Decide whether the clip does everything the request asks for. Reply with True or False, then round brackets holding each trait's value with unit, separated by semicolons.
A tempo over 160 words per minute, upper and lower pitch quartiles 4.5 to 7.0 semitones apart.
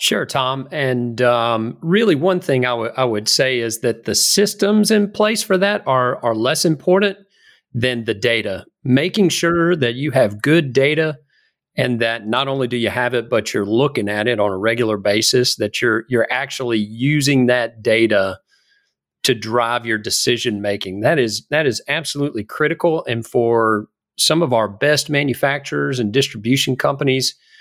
True (170 wpm; 5.3 semitones)